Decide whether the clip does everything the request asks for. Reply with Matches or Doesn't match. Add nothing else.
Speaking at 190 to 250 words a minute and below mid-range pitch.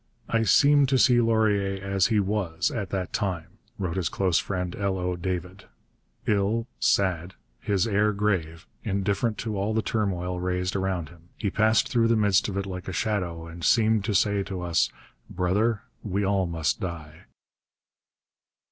Doesn't match